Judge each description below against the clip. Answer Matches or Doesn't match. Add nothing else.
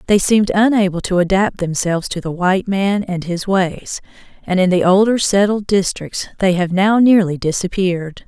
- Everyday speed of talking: Matches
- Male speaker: Doesn't match